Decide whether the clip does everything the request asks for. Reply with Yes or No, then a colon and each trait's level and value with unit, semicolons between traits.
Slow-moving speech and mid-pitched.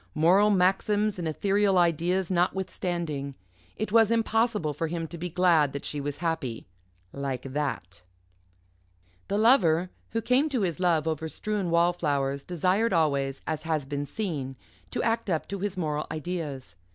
No: average, 150 wpm; medium, 170 Hz